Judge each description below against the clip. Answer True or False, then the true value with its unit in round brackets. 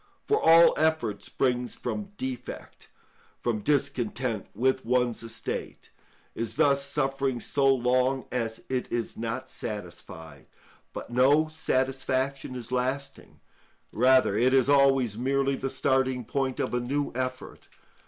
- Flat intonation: True (2.3 semitones)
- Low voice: True (130 Hz)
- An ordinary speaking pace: False (120 wpm)